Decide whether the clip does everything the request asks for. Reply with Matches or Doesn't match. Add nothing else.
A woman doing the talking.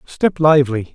Doesn't match